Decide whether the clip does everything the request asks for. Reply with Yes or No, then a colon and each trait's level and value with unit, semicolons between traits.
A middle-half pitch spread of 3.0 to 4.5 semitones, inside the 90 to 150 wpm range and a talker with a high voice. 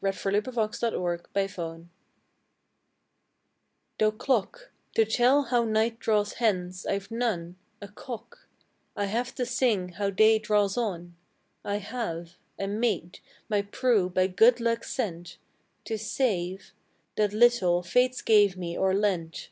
Yes: average, 4.2 semitones; slow, 135 wpm; high, 205 Hz